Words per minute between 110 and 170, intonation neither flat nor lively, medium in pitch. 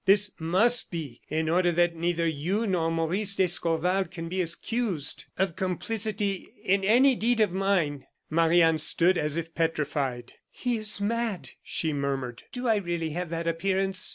Yes: average, 160 wpm; average, 3.5 semitones; medium, 175 Hz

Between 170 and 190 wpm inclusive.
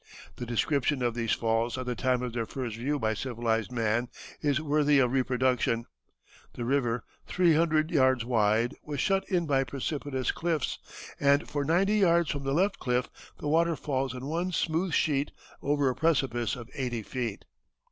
Yes: average, 175 wpm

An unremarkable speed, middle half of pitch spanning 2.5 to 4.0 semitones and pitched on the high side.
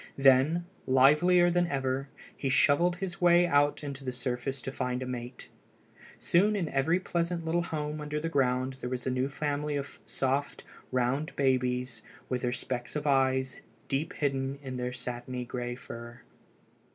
No: average, 165 wpm; average, 3.1 semitones; low, 135 Hz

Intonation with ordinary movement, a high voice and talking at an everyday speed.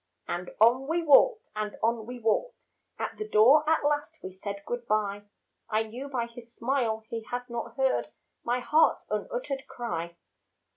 Yes: average, 4.1 semitones; high, 240 Hz; average, 165 wpm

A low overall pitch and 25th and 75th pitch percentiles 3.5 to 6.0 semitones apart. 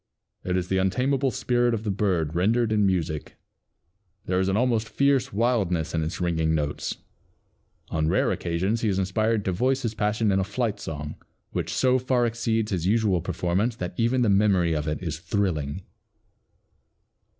Yes: low, 100 Hz; average, 4.8 semitones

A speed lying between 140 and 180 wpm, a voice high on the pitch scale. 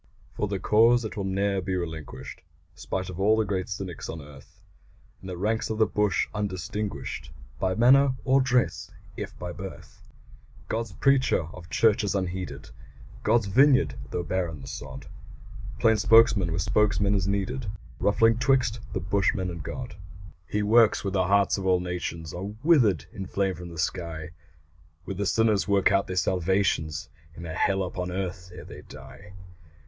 No: average, 170 wpm; very low, 95 Hz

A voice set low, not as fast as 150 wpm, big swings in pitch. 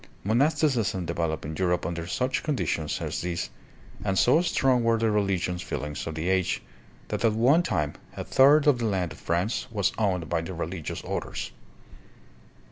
No: very low, 95 Hz; average, 175 wpm; wide, 6.1 semitones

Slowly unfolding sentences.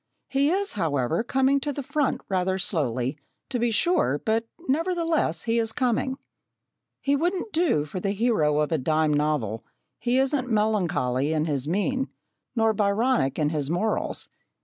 No: average, 155 wpm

